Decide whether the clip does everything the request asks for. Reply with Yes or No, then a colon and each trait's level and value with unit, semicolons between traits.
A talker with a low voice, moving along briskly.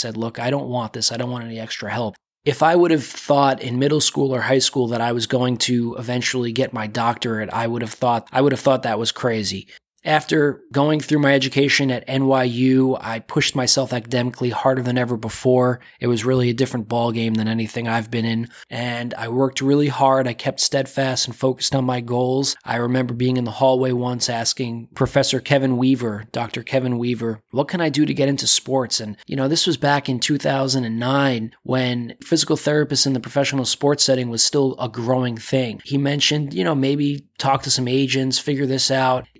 Yes: low, 130 Hz; fast, 210 wpm